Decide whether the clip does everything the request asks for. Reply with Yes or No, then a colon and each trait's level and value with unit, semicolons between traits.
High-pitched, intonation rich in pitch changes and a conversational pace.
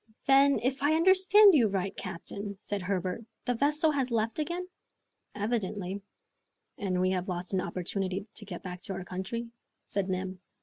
Yes: high, 200 Hz; wide, 6.5 semitones; average, 165 wpm